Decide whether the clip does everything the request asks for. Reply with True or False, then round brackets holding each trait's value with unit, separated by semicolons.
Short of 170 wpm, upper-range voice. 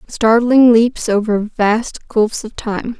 True (140 wpm; 225 Hz)